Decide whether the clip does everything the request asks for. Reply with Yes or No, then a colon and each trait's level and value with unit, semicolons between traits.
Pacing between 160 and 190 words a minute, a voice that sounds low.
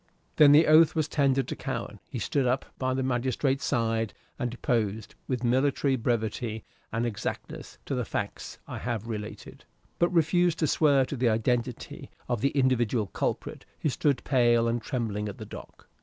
Yes: average, 170 wpm; low, 125 Hz